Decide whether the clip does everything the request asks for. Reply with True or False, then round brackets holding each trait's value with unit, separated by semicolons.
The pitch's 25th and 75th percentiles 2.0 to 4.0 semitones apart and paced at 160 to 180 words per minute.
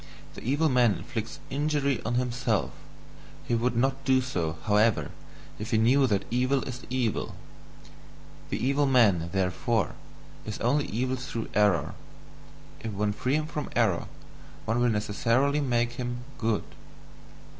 False (3.4 semitones; 140 wpm)